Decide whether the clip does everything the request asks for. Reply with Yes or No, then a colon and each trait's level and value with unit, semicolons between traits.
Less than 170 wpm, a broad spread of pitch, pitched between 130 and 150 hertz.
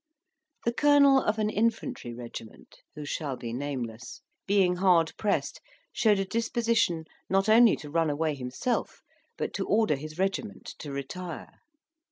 No: average, 145 wpm; wide, 7.3 semitones; medium, 180 Hz